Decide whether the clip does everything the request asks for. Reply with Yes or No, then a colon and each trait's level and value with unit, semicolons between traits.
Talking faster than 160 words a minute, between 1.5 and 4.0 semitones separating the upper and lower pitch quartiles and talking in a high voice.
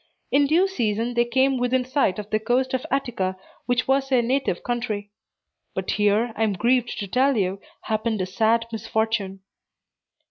Yes: average, 170 wpm; average, 3.6 semitones; high, 235 Hz